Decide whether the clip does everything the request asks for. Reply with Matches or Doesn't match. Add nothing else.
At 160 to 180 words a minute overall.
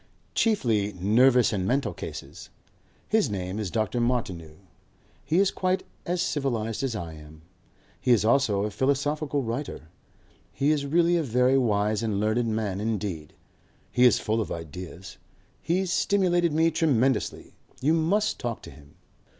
Doesn't match